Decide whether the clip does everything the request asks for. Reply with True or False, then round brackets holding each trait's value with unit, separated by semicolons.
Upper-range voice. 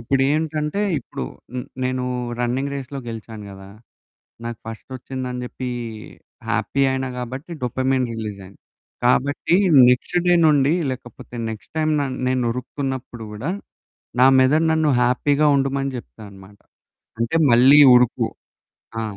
False (130 Hz)